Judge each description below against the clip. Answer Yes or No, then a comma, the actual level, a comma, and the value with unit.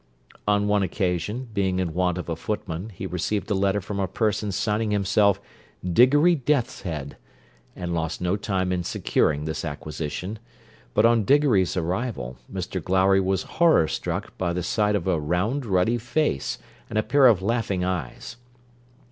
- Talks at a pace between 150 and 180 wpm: Yes, average, 160 wpm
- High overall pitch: No, very low, 95 Hz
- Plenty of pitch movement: No, average, 3.5 semitones